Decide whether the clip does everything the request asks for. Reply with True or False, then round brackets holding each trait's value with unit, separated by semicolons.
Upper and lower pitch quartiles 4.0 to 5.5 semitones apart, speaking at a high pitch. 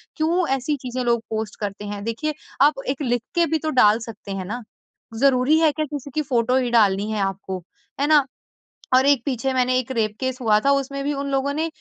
True (4.3 semitones; 255 Hz)